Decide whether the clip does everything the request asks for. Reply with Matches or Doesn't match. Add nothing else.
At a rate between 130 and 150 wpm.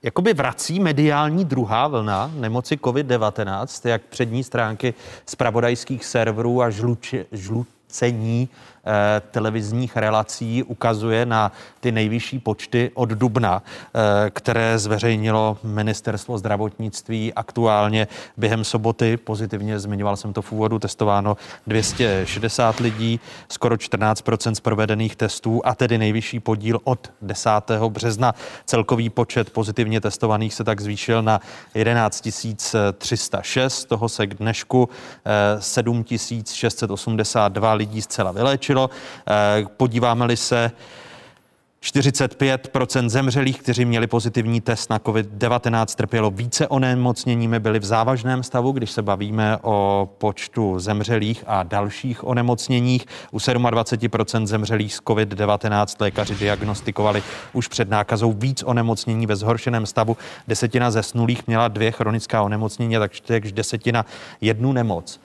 Doesn't match